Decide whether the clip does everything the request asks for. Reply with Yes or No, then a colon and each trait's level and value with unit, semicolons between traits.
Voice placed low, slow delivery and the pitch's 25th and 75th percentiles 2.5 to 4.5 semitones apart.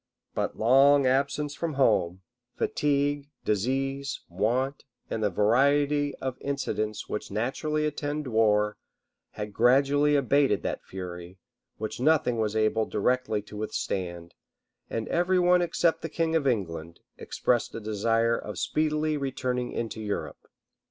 No: low, 130 Hz; slow, 130 wpm; average, 5.2 semitones